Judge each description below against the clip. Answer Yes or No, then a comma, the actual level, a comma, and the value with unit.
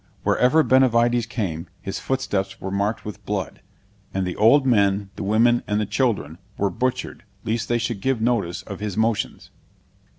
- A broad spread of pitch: No, average, 3.5 semitones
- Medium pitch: No, low, 110 Hz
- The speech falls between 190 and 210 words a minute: No, average, 165 wpm